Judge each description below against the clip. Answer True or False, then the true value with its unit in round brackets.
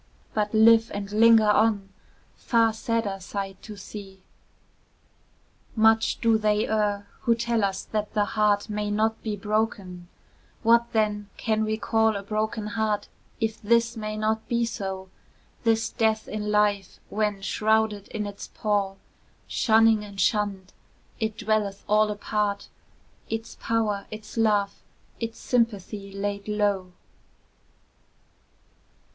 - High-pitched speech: True (215 Hz)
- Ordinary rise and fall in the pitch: False (1.5 semitones)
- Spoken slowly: True (130 wpm)